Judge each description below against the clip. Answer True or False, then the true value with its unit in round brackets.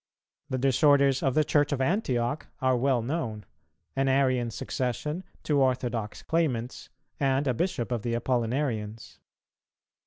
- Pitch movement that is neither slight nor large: True (3.0 semitones)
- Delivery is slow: True (130 wpm)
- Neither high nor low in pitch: False (130 Hz)